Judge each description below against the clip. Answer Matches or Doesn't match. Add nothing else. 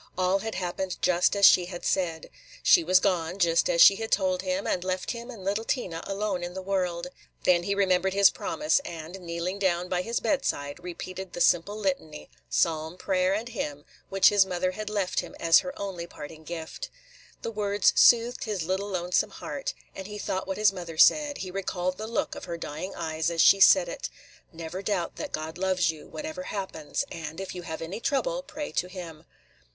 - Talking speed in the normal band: Doesn't match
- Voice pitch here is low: Doesn't match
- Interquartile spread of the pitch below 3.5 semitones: Matches